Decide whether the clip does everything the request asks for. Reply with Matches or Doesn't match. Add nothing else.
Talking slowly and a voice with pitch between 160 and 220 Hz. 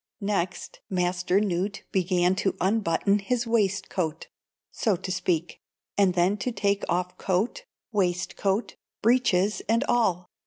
Matches